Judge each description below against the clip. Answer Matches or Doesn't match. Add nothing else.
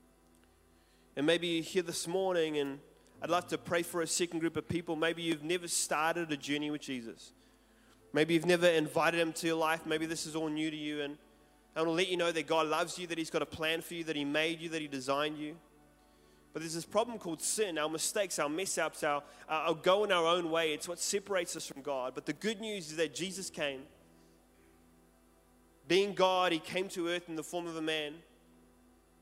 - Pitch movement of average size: Matches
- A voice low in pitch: Doesn't match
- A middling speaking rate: Doesn't match